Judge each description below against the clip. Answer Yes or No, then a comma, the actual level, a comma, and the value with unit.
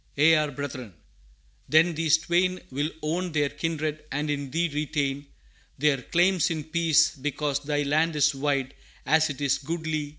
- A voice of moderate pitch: Yes, medium, 150 Hz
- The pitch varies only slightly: Yes, narrow, 2.0 semitones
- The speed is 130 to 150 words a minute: No, average, 160 wpm